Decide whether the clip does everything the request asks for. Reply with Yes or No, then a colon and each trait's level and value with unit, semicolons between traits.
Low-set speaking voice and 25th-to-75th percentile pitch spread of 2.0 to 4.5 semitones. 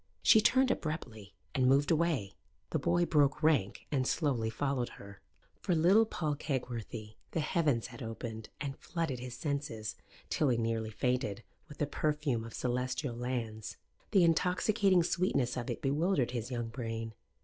No: low, 130 Hz; average, 5.3 semitones